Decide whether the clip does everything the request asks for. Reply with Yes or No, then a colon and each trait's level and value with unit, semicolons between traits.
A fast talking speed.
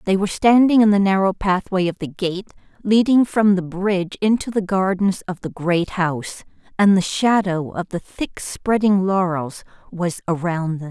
No: average, 175 wpm